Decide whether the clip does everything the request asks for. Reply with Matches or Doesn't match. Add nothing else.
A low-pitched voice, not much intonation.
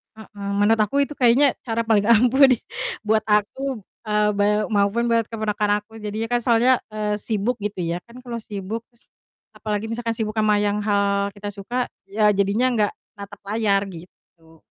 Doesn't match